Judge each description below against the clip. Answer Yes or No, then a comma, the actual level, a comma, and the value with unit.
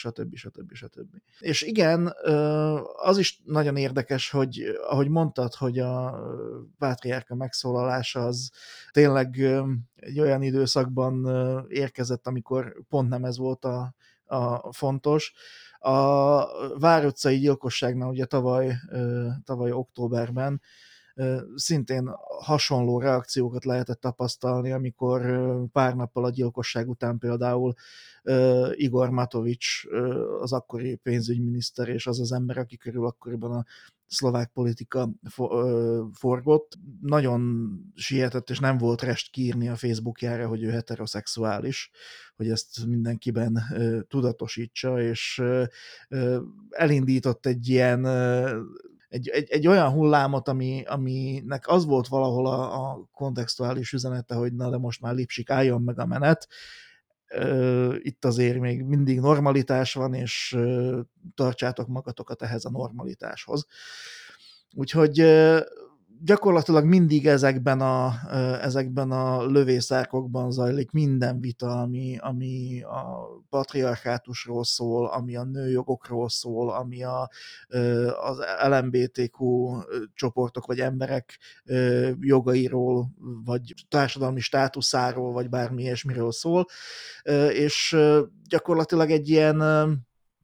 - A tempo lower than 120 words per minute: Yes, slow, 105 wpm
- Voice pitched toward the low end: Yes, low, 130 Hz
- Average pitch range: No, narrow, 1.9 semitones